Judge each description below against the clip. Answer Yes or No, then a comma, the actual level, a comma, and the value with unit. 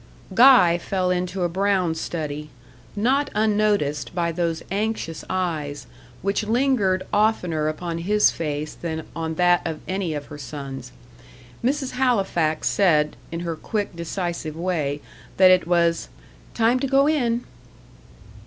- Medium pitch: Yes, medium, 175 Hz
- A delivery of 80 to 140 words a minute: Yes, slow, 135 wpm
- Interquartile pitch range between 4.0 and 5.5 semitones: Yes, average, 4.7 semitones